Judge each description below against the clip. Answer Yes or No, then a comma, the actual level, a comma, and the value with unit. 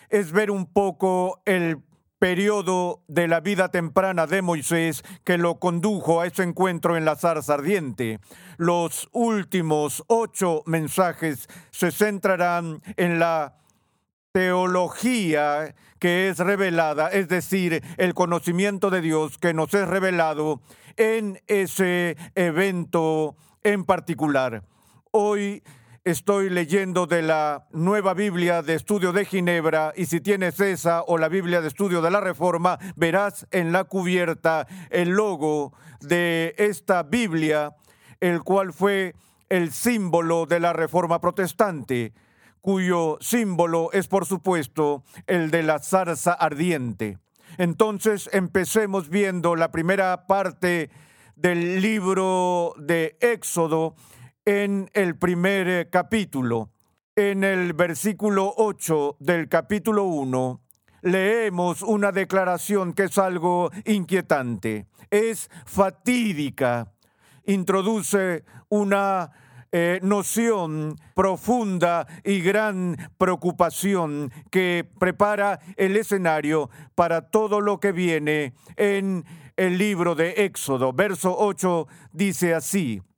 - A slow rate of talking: Yes, slow, 115 wpm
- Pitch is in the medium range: Yes, medium, 180 Hz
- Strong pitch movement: No, average, 3.2 semitones